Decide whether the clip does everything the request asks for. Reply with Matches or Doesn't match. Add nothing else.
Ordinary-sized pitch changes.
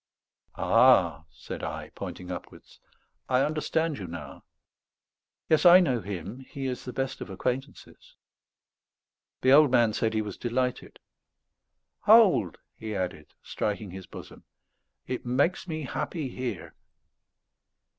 Doesn't match